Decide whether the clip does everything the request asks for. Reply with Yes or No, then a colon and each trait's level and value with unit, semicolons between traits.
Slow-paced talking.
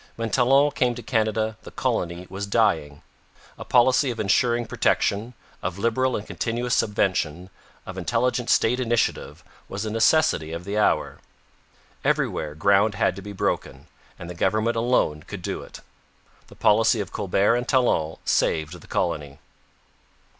No: average, 150 wpm